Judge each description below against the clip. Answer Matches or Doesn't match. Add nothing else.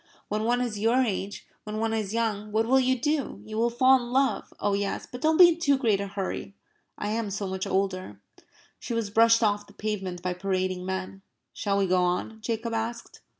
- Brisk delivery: Matches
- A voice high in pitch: Matches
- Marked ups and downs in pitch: Doesn't match